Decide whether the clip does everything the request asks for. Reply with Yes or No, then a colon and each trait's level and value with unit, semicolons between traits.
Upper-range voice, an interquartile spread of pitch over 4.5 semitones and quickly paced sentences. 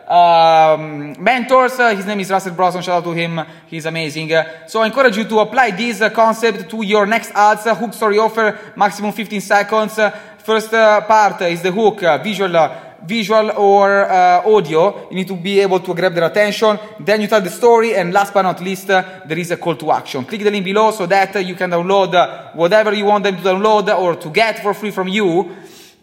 No: high, 205 Hz; average, 3.1 semitones; fast, 230 wpm